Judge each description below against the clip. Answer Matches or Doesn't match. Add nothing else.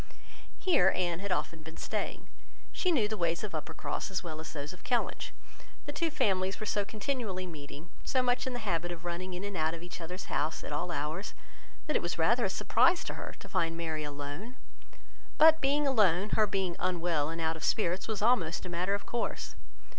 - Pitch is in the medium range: Matches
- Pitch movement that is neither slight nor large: Matches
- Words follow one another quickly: Matches